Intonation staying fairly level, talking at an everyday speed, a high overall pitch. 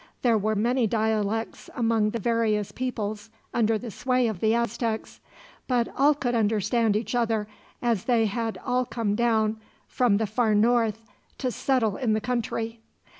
Yes: narrow, 1.9 semitones; average, 160 wpm; high, 225 Hz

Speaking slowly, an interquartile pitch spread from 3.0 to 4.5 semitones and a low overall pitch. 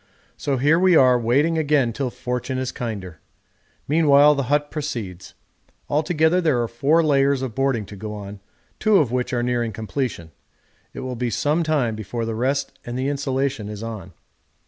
No: average, 175 wpm; average, 4.2 semitones; low, 130 Hz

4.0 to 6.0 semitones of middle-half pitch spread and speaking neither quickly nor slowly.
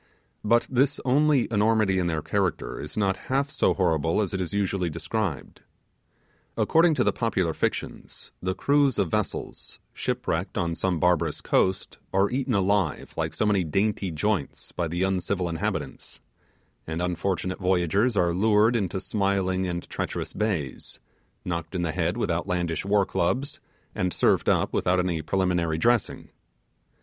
No: average, 3.5 semitones; average, 150 wpm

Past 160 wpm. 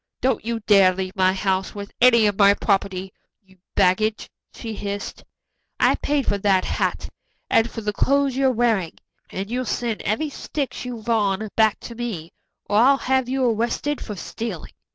Yes: average, 175 wpm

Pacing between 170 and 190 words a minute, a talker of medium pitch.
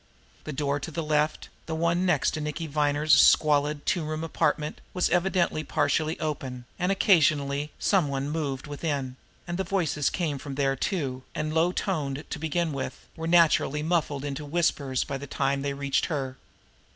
Yes: average, 175 wpm; medium, 150 Hz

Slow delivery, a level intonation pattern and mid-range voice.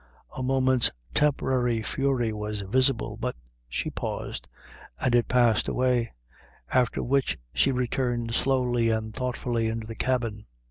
No: slow, 130 wpm; narrow, 2.3 semitones; low, 120 Hz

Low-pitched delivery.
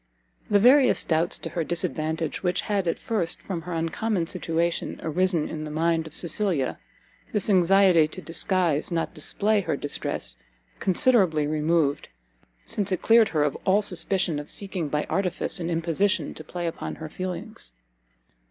No: medium, 170 Hz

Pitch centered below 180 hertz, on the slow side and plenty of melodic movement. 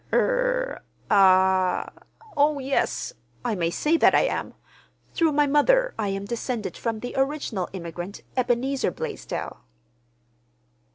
No: high, 245 Hz; slow, 110 wpm; wide, 7.4 semitones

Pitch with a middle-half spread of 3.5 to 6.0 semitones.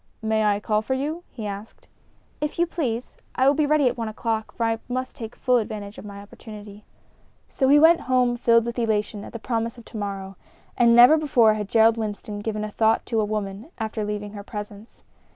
No: average, 2.8 semitones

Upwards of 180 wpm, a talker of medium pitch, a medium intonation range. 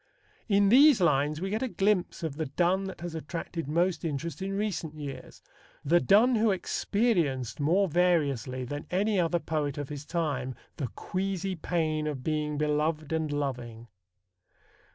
No: average, 155 wpm; medium, 160 Hz; average, 4.6 semitones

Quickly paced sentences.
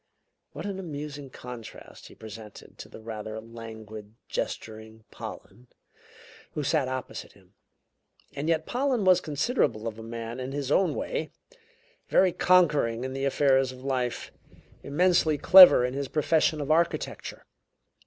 No: average, 140 wpm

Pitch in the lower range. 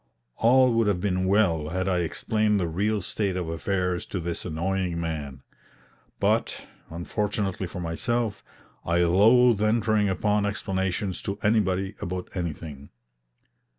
Yes: very low, 95 Hz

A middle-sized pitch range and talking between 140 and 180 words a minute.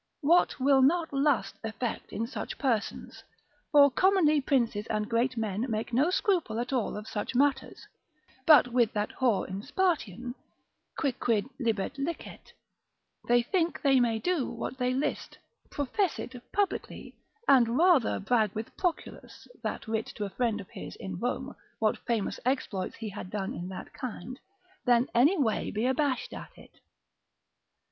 Yes: average, 4.4 semitones; average, 155 wpm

